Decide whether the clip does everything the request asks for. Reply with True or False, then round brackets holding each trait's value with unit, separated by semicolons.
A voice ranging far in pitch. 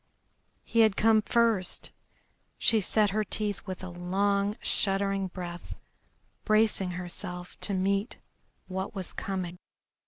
False (2.6 semitones)